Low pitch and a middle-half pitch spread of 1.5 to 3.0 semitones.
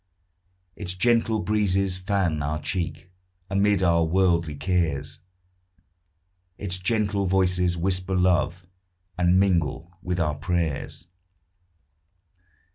Yes: very low, 90 Hz; narrow, 2.4 semitones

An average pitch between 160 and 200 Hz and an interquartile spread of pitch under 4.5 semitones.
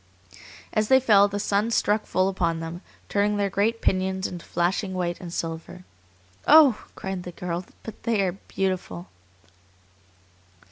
Yes: high, 190 Hz; average, 2.8 semitones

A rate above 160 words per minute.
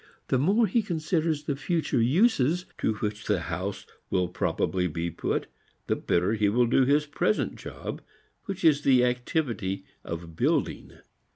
No: average, 155 wpm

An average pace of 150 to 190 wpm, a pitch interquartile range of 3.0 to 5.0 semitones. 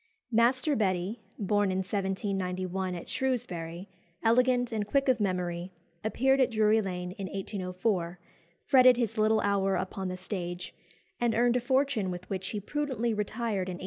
Yes: average, 155 wpm; average, 4.4 semitones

